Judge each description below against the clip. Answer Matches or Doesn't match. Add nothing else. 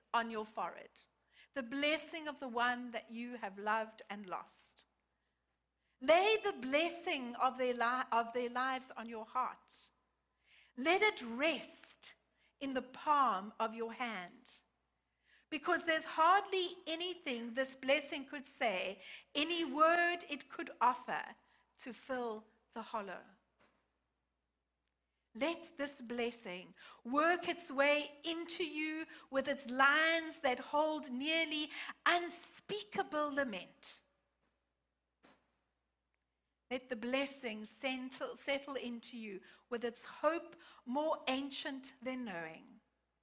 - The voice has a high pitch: Matches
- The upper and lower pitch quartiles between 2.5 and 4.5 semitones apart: Doesn't match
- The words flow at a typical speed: Doesn't match